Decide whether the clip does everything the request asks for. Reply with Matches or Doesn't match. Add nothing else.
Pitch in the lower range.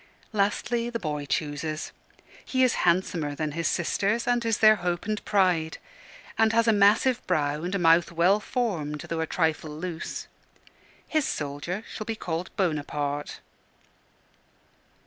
Doesn't match